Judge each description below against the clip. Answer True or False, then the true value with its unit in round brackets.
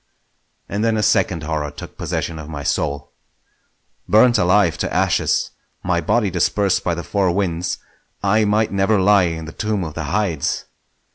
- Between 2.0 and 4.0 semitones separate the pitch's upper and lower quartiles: False (4.4 semitones)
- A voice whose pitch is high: False (90 Hz)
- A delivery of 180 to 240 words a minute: False (165 wpm)